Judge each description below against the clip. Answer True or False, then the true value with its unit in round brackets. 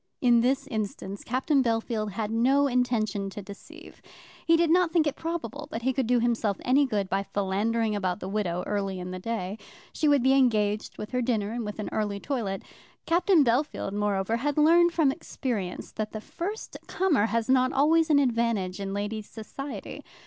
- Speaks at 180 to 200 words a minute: True (185 wpm)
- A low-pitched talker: False (230 Hz)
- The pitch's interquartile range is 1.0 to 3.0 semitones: False (5.0 semitones)